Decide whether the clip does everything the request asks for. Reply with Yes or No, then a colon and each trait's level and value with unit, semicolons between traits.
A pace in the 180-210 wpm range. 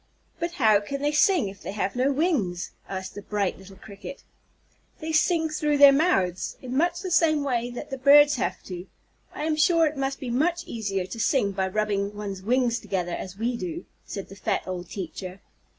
Yes: average, 200 wpm